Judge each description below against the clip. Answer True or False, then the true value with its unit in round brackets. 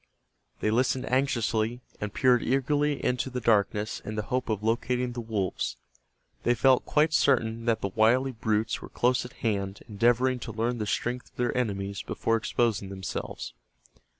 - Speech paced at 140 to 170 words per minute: True (165 wpm)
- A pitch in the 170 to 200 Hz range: False (115 Hz)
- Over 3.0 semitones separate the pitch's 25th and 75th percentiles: False (2.7 semitones)